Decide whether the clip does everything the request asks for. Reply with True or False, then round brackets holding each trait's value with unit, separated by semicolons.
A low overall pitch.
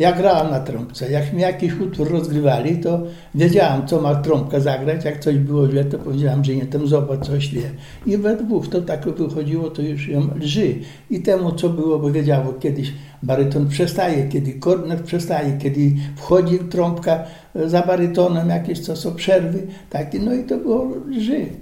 False (160 Hz)